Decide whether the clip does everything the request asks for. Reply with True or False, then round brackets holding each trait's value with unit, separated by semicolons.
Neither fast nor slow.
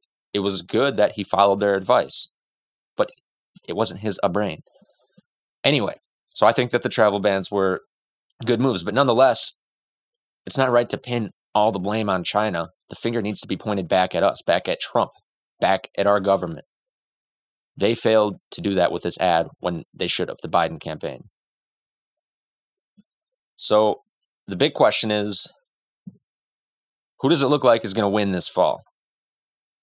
True (170 wpm)